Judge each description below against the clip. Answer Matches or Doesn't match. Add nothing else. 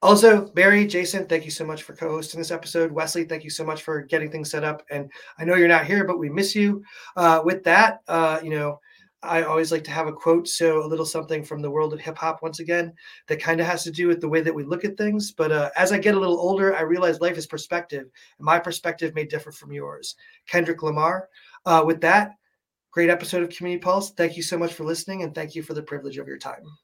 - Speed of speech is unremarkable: Doesn't match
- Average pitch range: Doesn't match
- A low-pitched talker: Doesn't match